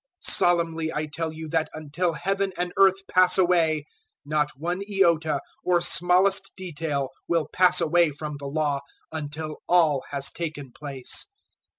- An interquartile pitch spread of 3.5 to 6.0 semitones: No, average, 2.9 semitones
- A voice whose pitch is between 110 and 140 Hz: No, medium, 160 Hz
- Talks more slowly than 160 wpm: Yes, average, 150 wpm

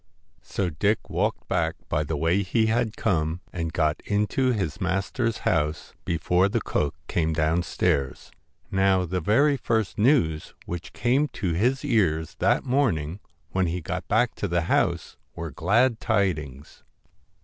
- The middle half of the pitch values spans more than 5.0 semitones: Yes, wide, 5.4 semitones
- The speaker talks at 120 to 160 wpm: Yes, average, 150 wpm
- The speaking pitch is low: Yes, very low, 90 Hz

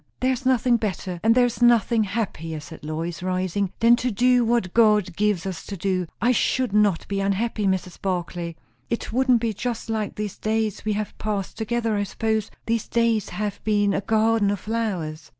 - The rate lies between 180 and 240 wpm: Yes, average, 190 wpm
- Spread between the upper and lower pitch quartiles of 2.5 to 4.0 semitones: Yes, average, 3.4 semitones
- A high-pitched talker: Yes, high, 210 Hz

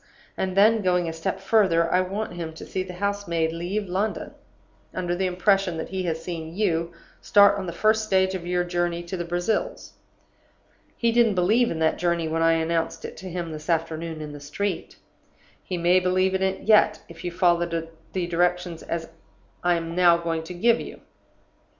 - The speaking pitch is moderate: Yes, medium, 175 Hz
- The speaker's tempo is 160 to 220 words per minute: Yes, average, 195 wpm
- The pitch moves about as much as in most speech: No, narrow, 2.3 semitones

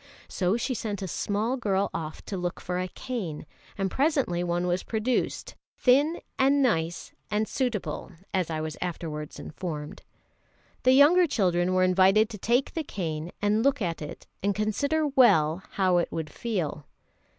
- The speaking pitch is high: Yes, high, 195 Hz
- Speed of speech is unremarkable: Yes, average, 160 wpm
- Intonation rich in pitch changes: Yes, wide, 5.9 semitones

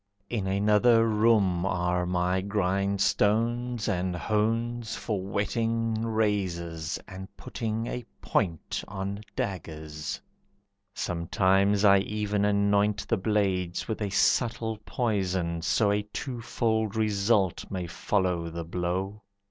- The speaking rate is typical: No, slow, 110 wpm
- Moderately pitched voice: No, low, 100 Hz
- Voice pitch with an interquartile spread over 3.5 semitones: No, average, 3.1 semitones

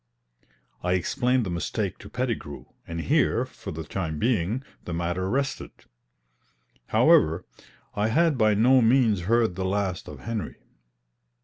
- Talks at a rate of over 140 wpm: No, slow, 135 wpm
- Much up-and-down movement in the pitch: Yes, wide, 5.9 semitones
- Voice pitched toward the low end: Yes, low, 105 Hz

